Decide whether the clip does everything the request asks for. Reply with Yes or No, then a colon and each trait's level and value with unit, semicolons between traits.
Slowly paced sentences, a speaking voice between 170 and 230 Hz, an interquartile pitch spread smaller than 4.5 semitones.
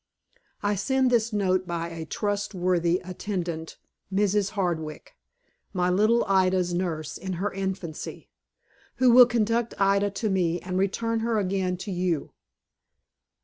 Yes: slow, 130 wpm; high, 190 Hz; average, 2.7 semitones